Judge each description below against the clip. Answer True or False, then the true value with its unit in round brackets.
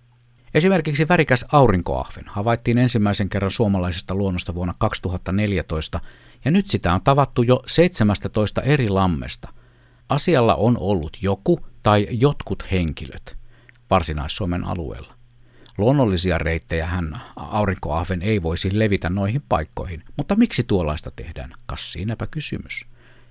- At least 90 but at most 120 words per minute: True (115 wpm)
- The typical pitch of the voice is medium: False (105 Hz)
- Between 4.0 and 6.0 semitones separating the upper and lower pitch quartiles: True (5.2 semitones)